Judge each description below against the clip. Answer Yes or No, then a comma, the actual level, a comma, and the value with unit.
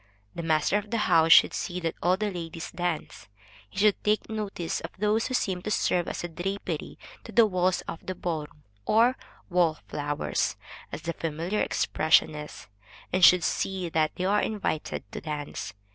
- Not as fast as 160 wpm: No, average, 180 wpm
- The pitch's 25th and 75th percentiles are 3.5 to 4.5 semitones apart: Yes, average, 4.0 semitones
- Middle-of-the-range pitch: Yes, medium, 180 Hz